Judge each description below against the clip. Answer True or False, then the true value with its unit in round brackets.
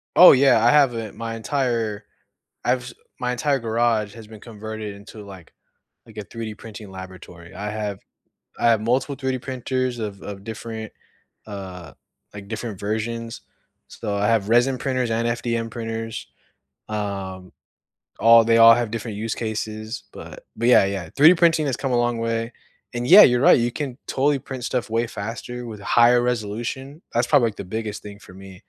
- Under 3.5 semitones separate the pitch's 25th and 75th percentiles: True (2.7 semitones)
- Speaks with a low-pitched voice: True (115 Hz)